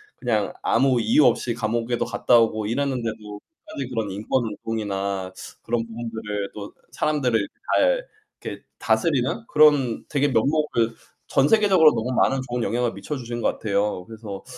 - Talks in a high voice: No, low, 115 Hz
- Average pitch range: Yes, average, 3.6 semitones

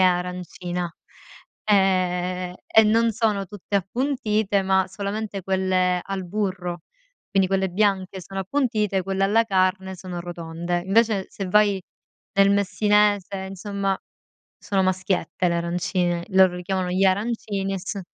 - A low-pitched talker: No, high, 190 Hz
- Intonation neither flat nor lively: No, narrow, 1.9 semitones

